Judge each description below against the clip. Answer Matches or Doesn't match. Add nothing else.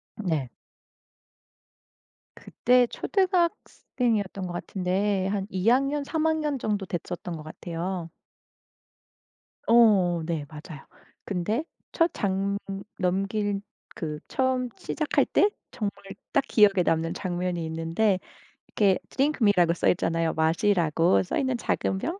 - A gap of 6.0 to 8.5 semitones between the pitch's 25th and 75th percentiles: Doesn't match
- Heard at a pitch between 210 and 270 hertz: Doesn't match